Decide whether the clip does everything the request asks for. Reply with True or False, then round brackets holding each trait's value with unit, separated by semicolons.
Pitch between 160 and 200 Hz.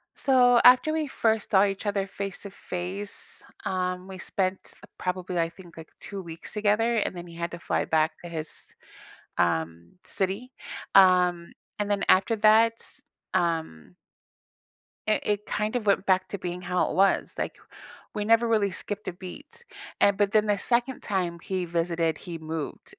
True (190 Hz)